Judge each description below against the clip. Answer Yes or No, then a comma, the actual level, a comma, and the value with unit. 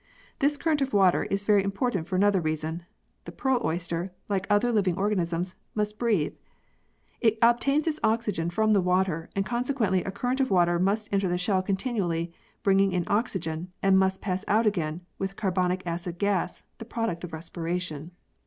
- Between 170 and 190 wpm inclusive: Yes, average, 175 wpm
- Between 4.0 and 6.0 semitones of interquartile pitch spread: No, average, 3.5 semitones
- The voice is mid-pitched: No, high, 195 Hz